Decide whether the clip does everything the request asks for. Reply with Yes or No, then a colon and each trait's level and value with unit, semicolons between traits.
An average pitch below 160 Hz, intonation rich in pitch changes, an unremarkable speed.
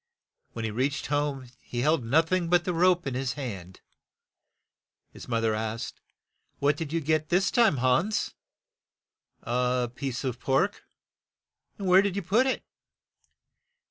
Yes: medium, 140 Hz; wide, 6.1 semitones; average, 160 wpm